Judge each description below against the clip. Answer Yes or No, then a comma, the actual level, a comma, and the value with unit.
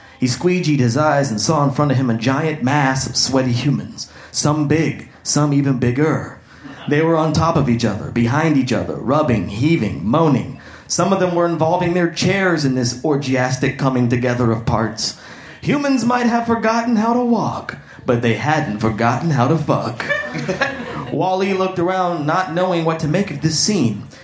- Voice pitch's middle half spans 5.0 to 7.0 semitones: Yes, average, 5.3 semitones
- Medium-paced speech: Yes, average, 180 wpm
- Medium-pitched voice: Yes, medium, 150 Hz